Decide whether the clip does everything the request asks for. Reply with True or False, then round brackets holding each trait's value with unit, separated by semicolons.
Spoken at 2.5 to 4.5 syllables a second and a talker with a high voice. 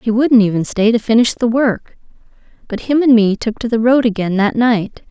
False (5.2 syllables/s; 230 Hz)